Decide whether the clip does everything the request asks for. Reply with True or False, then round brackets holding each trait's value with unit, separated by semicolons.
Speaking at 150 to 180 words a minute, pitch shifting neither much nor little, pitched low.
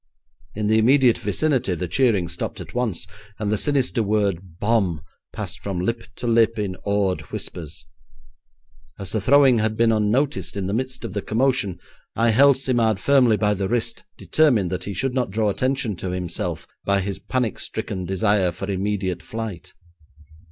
True (165 wpm; 4.0 semitones; 105 Hz)